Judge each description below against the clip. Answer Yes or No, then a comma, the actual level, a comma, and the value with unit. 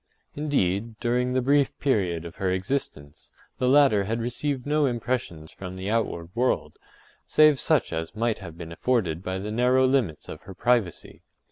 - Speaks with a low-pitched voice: Yes, low, 115 Hz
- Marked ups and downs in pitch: Yes, wide, 5.8 semitones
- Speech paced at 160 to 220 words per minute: Yes, average, 165 wpm